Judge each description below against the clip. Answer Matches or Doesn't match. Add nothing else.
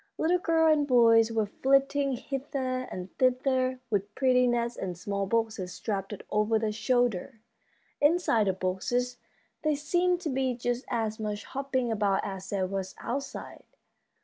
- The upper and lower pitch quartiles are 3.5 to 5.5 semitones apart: Matches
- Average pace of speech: Matches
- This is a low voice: Doesn't match